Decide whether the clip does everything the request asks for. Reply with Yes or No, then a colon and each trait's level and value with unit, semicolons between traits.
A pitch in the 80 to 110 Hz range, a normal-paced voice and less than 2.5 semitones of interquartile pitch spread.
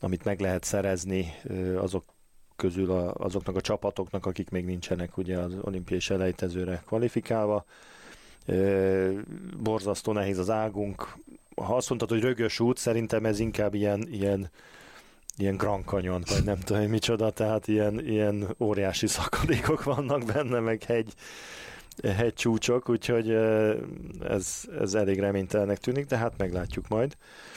No: low, 105 Hz; average, 135 wpm; average, 2.8 semitones